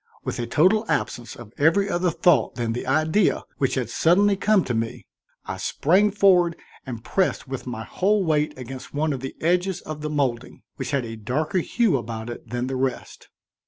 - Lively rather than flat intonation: Yes, wide, 6.6 semitones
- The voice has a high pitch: No, medium, 150 Hz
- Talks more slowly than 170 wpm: No, average, 195 wpm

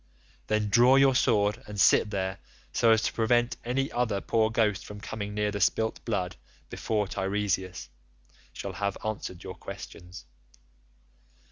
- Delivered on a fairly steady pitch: Yes, narrow, 2.2 semitones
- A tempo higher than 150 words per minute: No, average, 145 wpm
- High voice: No, low, 105 Hz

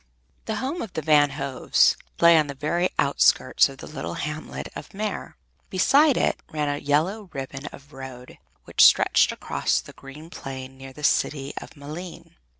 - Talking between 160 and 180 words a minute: Yes, average, 175 wpm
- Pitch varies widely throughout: No, average, 4.0 semitones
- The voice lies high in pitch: No, medium, 150 Hz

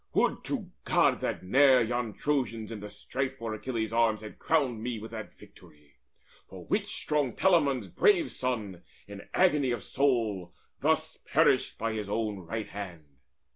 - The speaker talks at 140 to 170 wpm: Yes, average, 160 wpm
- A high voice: No, low, 115 Hz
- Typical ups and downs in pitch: Yes, average, 4.2 semitones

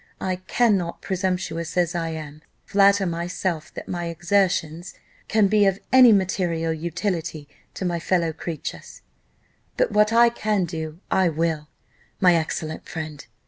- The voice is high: No, medium, 175 Hz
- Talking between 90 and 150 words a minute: Yes, average, 140 wpm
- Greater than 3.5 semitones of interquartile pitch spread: No, average, 3.2 semitones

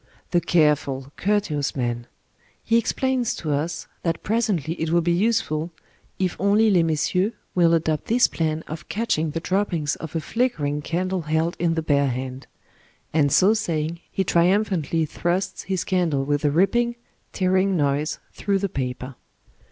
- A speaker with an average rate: Yes, average, 160 wpm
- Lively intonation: No, average, 4.3 semitones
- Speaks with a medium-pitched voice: Yes, medium, 165 Hz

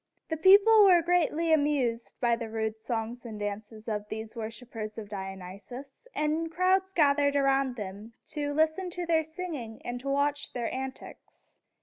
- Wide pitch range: Yes, wide, 6.2 semitones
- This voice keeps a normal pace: Yes, average, 155 wpm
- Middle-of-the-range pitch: No, very high, 265 Hz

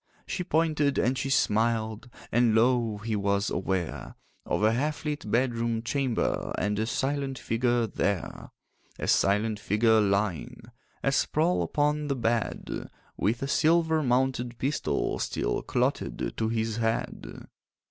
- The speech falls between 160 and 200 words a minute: No, slow, 135 wpm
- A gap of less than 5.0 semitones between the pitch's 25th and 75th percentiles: Yes, average, 4.0 semitones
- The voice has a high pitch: No, low, 115 Hz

